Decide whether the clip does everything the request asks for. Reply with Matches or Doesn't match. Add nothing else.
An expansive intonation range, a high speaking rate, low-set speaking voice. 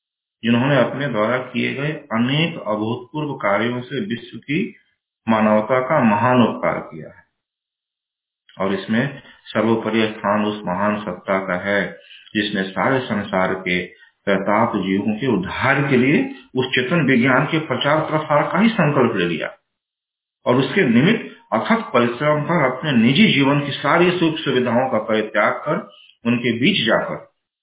Doesn't match